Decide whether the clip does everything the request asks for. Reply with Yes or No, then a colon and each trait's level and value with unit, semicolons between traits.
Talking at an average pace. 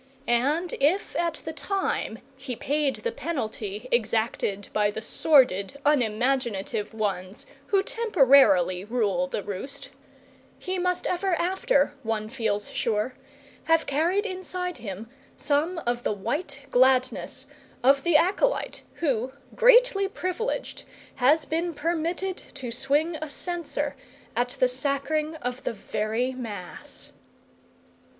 No: slow, 120 wpm